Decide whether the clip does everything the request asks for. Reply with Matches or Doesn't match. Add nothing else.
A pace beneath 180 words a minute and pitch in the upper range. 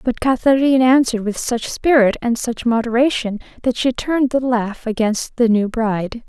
Matches